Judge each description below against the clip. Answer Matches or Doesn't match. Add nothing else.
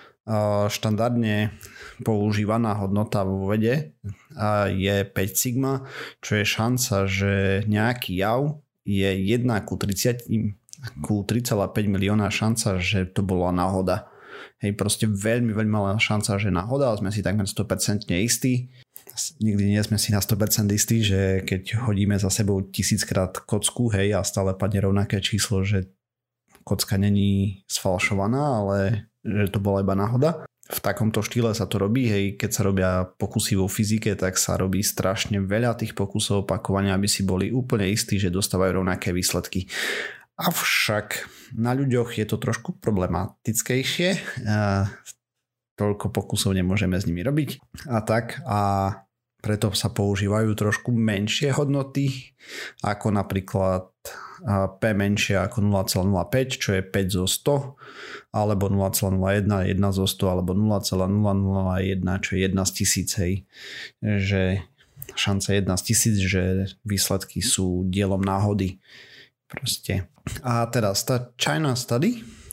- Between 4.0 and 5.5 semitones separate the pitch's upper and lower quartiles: Doesn't match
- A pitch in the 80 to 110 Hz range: Matches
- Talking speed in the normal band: Matches